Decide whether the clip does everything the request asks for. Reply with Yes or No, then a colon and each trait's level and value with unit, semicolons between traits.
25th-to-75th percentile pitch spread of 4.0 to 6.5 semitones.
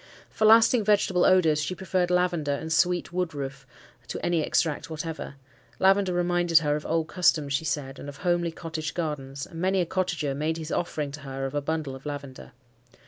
No: average, 3.5 semitones